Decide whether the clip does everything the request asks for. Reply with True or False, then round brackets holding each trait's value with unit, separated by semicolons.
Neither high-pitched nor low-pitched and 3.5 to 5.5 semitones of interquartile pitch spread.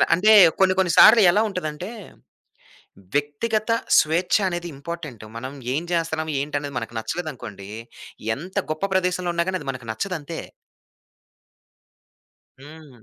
True (165 Hz; 4.1 semitones)